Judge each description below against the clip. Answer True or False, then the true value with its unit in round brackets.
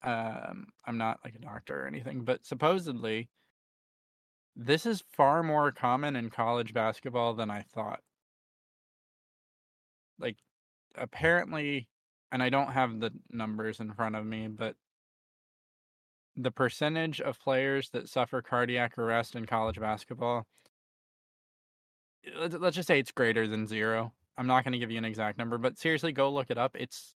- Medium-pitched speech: False (120 Hz)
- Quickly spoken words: False (150 wpm)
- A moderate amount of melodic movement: True (3.7 semitones)